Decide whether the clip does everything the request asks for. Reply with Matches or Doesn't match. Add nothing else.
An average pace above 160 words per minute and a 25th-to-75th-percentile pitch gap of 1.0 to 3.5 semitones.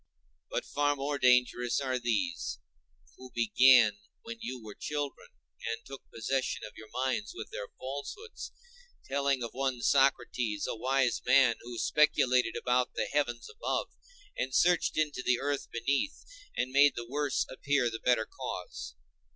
Doesn't match